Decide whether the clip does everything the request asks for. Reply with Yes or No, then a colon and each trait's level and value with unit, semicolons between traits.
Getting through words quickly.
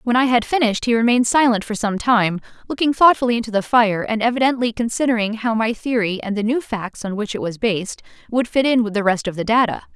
Yes: fast, 235 wpm